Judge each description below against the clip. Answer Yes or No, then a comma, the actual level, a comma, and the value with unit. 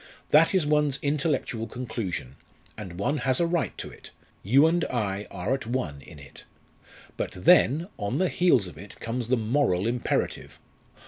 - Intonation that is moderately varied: No, wide, 6.7 semitones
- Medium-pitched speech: No, low, 125 Hz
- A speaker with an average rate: Yes, average, 170 wpm